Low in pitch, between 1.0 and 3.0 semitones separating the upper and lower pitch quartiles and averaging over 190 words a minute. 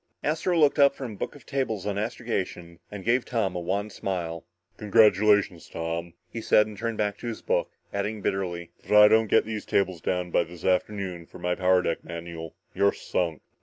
No: low, 100 Hz; average, 3.8 semitones; fast, 205 wpm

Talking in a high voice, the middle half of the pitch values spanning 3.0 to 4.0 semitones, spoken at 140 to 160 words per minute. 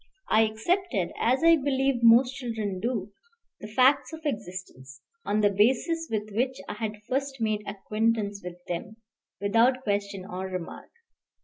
No: high, 220 Hz; average, 4.4 semitones; average, 145 wpm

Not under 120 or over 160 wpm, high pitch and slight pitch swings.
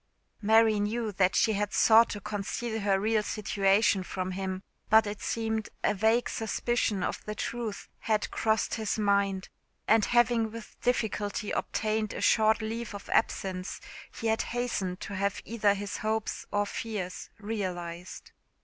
Yes: average, 150 wpm; high, 210 Hz; narrow, 2.0 semitones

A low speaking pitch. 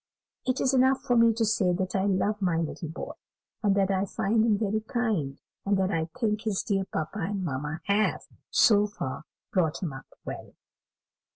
No: high, 200 Hz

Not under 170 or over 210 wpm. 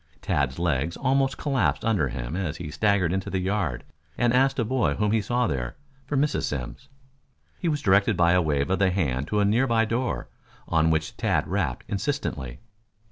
Yes: average, 190 wpm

